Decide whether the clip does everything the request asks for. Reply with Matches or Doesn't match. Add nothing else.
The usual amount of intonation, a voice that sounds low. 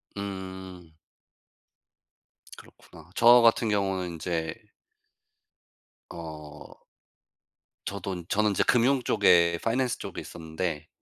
Matches